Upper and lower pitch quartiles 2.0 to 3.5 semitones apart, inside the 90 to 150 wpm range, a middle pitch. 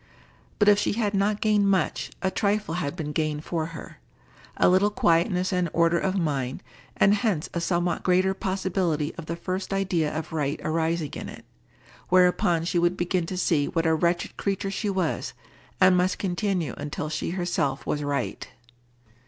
No: average, 3.0 semitones; average, 175 wpm; medium, 175 Hz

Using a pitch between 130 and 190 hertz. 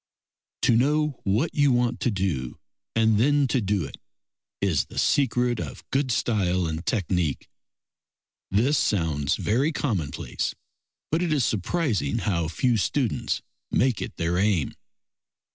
No: low, 110 Hz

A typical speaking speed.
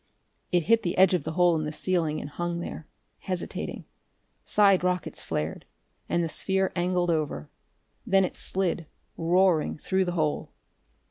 Yes: average, 155 wpm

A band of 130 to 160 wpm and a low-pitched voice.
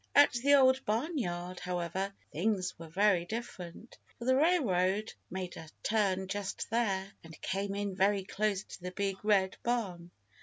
No: average, 155 wpm; high, 195 Hz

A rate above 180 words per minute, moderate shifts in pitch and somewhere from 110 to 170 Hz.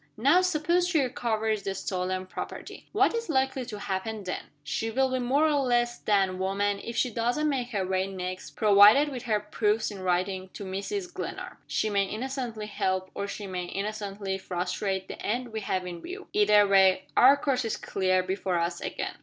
No: average, 190 wpm; average, 4.9 semitones; high, 210 Hz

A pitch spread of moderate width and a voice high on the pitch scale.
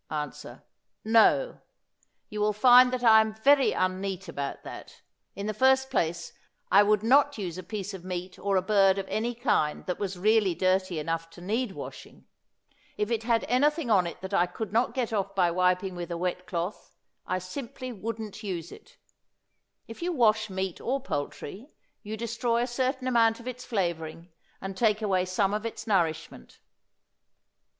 Yes: average, 4.2 semitones; high, 205 Hz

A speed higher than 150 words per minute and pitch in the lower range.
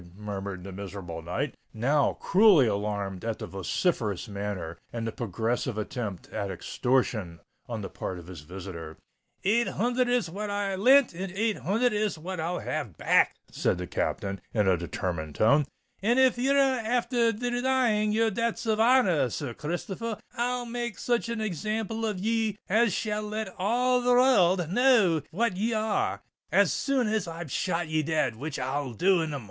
No: average, 175 wpm; medium, 180 Hz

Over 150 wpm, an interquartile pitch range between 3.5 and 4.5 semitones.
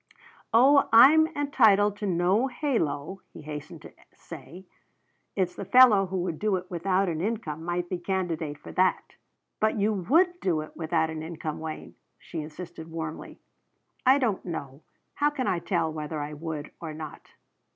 No: average, 165 wpm; average, 5.0 semitones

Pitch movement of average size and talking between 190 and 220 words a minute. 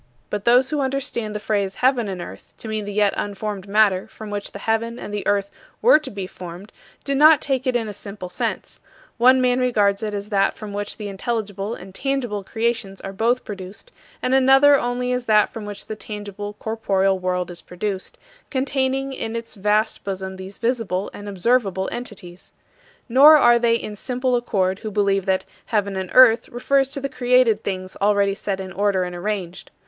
Yes: average, 3.9 semitones; average, 195 wpm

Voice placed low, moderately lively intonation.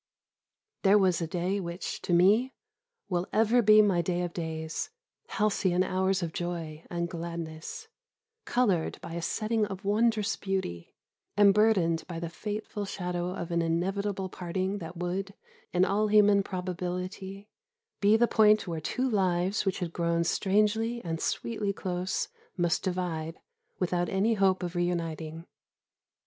No: medium, 185 Hz; average, 3.0 semitones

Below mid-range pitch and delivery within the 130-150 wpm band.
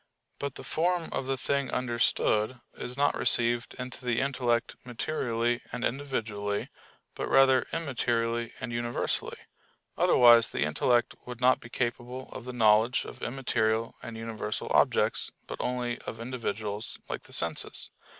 Yes: low, 120 Hz; average, 140 wpm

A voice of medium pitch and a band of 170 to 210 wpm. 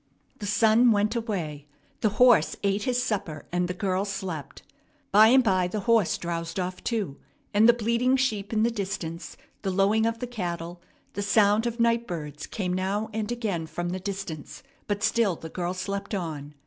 No: high, 200 Hz; average, 185 wpm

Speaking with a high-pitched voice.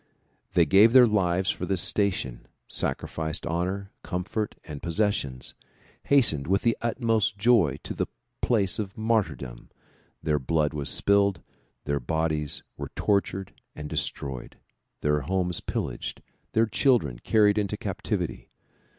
No: very low, 95 Hz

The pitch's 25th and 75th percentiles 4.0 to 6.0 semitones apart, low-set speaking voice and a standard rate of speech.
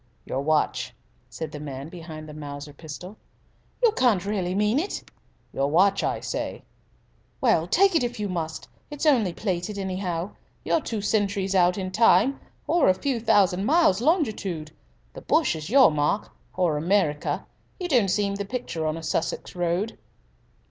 No: wide, 5.4 semitones; high, 190 Hz; average, 165 wpm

